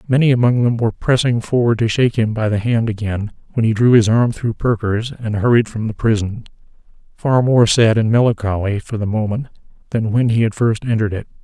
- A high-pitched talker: No, low, 115 Hz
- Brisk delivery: Yes, fast, 210 wpm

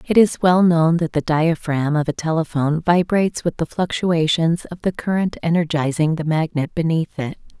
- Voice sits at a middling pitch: Yes, medium, 165 Hz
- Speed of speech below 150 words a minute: No, average, 175 wpm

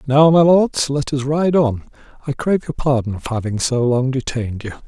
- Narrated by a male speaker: Yes, male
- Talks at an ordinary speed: No, fast, 210 wpm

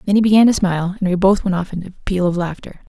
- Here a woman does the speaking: Yes, female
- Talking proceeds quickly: Yes, fast, 305 wpm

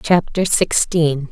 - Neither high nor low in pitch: Yes, medium, 160 Hz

